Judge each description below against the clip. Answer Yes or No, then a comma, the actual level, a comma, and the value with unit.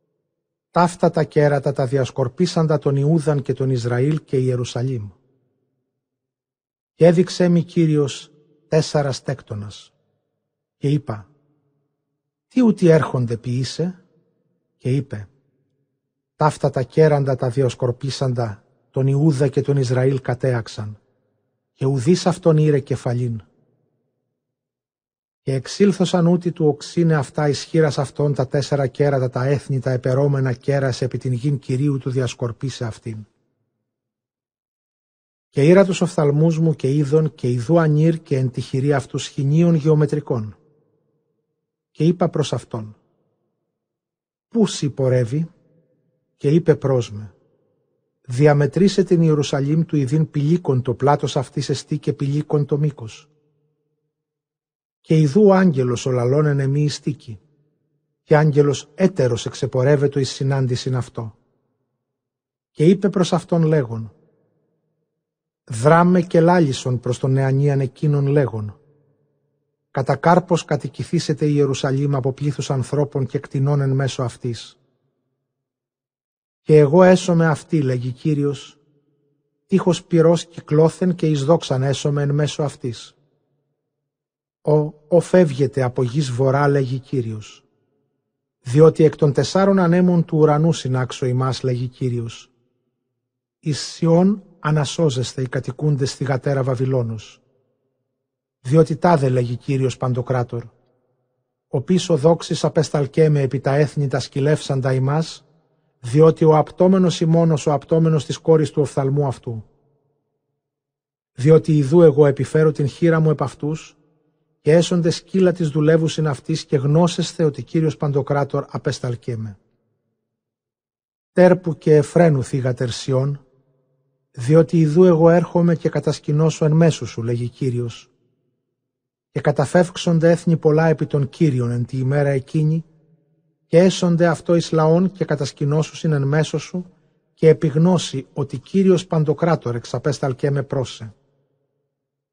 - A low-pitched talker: No, medium, 145 Hz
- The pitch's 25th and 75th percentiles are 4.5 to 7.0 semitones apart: No, average, 3.2 semitones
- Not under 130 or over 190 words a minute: No, average, 120 wpm